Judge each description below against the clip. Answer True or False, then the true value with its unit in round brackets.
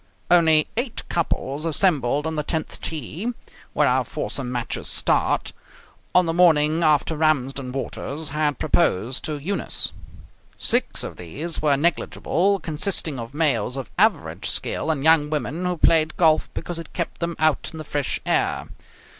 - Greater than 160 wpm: False (155 wpm)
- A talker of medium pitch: True (155 Hz)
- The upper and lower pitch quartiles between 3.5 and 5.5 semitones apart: False (2.9 semitones)